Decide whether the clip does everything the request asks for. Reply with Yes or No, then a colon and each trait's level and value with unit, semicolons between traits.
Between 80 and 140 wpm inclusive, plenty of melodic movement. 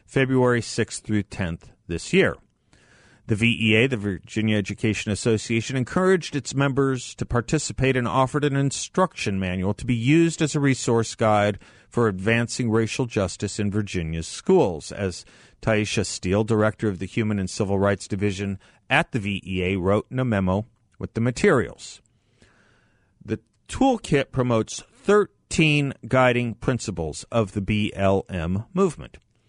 No: slow, 135 wpm; average, 4.3 semitones